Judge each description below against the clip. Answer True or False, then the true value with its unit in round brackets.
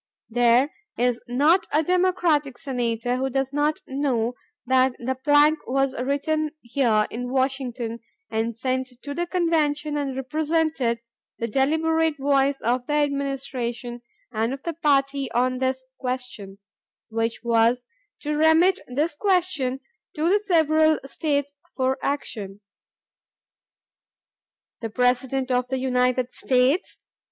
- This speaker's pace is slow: True (125 wpm)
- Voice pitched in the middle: False (265 Hz)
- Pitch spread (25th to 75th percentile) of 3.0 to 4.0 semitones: True (3.3 semitones)